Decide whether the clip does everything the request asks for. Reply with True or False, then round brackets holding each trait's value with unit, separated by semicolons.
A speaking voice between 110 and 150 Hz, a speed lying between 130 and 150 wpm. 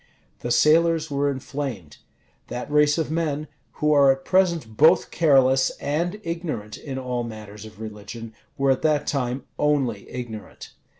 True (140 Hz; 145 wpm)